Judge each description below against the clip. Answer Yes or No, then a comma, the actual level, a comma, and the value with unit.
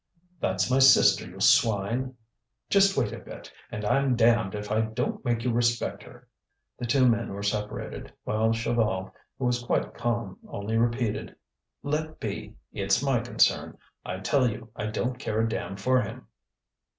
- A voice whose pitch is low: Yes, low, 115 Hz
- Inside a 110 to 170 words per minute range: Yes, average, 165 wpm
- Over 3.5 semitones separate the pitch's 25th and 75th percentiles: No, average, 2.8 semitones